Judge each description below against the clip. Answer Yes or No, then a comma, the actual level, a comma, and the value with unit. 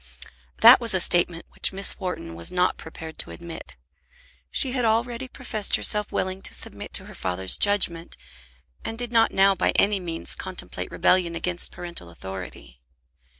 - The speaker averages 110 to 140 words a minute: No, average, 160 wpm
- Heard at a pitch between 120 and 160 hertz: No, medium, 185 Hz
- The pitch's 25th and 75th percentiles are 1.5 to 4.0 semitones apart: No, average, 4.8 semitones